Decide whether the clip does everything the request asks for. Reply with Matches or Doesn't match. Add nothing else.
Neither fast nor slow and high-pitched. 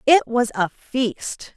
Matches